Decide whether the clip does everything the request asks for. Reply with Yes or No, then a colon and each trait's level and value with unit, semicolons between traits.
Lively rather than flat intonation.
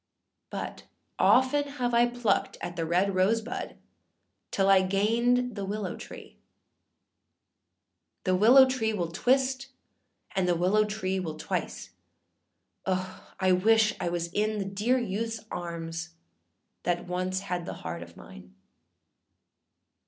No: average, 4.3 semitones